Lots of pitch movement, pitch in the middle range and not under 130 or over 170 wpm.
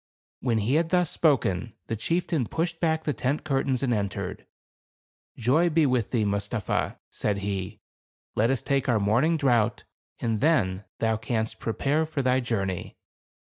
No: wide, 6.0 semitones; low, 125 Hz; average, 160 wpm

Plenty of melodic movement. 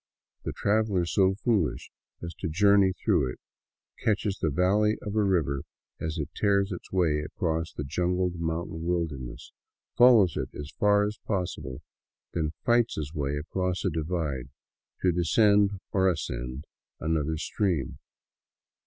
No: average, 4.5 semitones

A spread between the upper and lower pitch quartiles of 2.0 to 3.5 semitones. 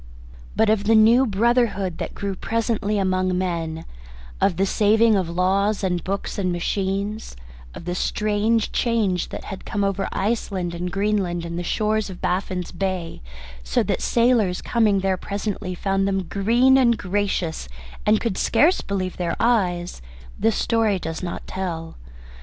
Yes: average, 3.1 semitones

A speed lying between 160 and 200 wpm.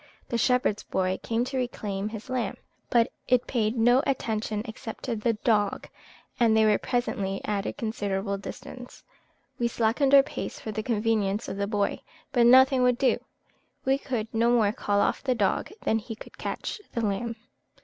Yes: average, 180 wpm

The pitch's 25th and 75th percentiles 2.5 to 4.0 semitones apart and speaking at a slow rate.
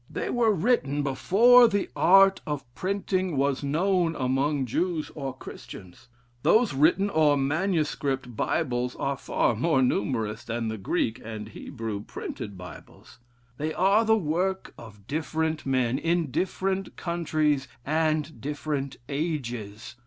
No: wide, 5.6 semitones; slow, 125 wpm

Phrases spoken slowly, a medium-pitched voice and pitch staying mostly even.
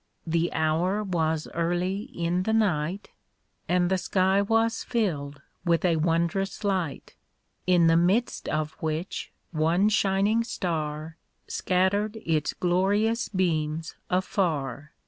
No: slow, 115 wpm; medium, 175 Hz; average, 3.5 semitones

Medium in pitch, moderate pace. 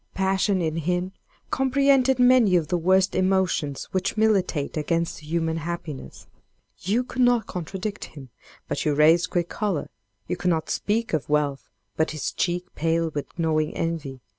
Yes: medium, 175 Hz; average, 155 wpm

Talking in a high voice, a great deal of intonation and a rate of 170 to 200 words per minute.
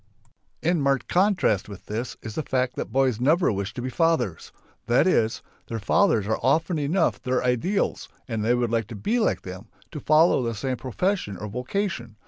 No: low, 125 Hz; wide, 6.4 semitones; average, 190 wpm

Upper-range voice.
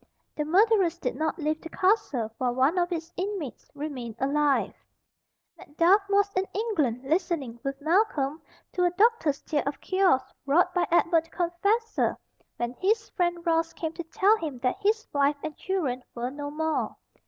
Yes: very high, 330 Hz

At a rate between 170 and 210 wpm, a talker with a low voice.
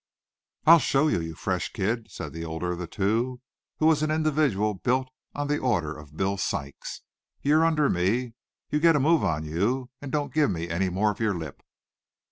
Yes: average, 200 wpm; low, 115 Hz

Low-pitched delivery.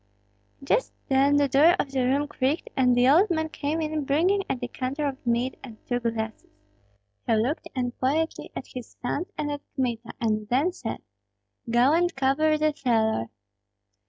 No: very high, 270 Hz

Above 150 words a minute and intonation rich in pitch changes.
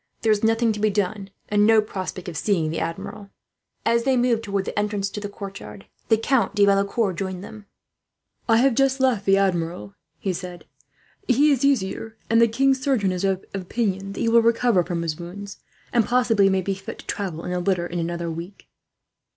No: fast, 205 wpm; average, 3.6 semitones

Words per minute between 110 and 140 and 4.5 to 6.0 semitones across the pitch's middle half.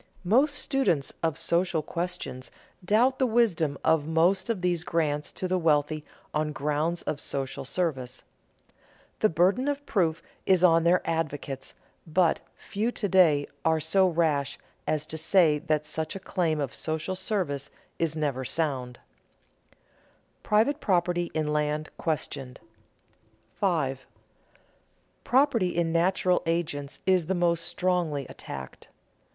No: slow, 135 wpm; average, 3.5 semitones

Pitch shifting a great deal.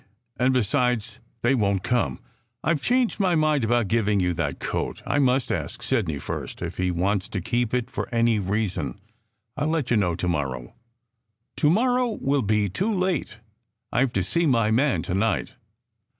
Yes: wide, 6.2 semitones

